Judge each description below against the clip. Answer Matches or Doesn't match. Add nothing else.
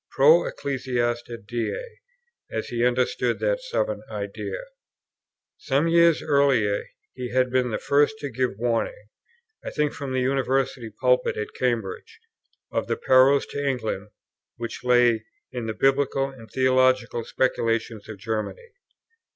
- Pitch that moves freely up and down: Doesn't match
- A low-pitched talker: Matches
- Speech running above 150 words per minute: Doesn't match